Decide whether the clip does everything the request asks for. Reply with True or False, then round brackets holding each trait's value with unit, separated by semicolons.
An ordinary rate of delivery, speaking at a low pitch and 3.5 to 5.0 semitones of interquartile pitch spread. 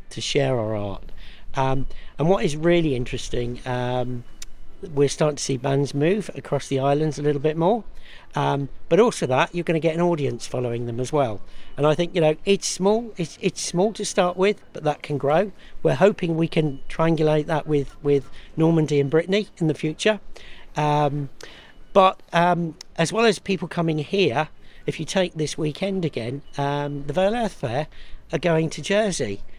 False (190 wpm; 155 Hz; 4.3 semitones)